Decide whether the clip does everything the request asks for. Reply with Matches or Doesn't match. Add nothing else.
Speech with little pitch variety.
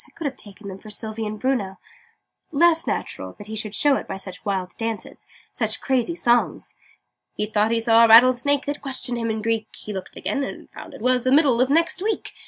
Doesn't match